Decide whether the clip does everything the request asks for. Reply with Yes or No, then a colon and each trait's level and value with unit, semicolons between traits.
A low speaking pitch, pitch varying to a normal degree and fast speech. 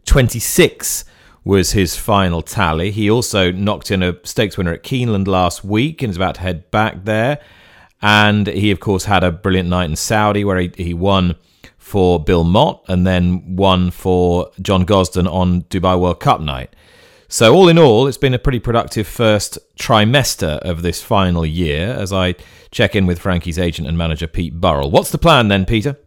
No: very low, 95 Hz; average, 3.1 semitones; average, 185 wpm